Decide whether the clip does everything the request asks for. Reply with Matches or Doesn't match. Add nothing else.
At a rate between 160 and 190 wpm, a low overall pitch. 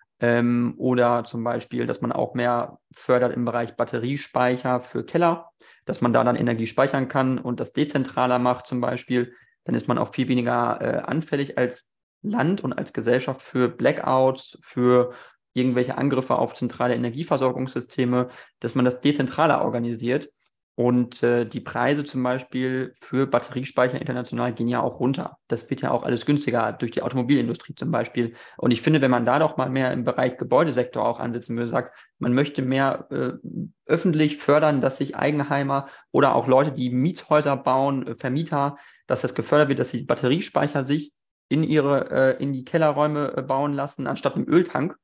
Matches